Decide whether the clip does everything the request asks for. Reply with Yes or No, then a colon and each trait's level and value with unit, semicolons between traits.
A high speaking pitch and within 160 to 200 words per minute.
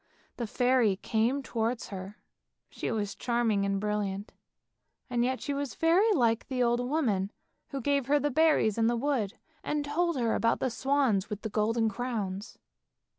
Yes: high, 235 Hz; average, 170 wpm